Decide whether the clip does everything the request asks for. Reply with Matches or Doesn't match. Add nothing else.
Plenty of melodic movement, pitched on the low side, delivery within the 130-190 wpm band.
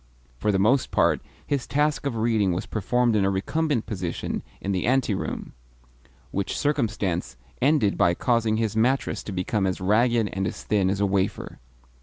Doesn't match